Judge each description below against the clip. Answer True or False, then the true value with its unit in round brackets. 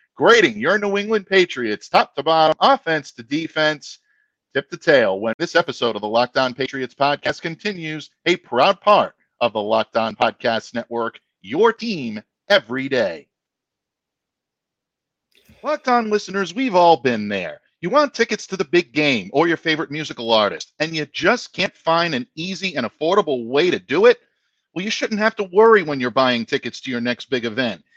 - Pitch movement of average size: False (8.3 semitones)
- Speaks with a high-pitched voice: False (165 Hz)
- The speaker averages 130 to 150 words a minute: False (175 wpm)